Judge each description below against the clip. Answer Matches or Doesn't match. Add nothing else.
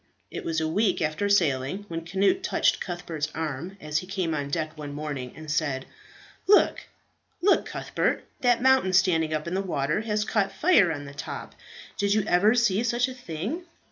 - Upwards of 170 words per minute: Matches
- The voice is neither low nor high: Matches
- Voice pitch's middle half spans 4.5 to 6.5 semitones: Matches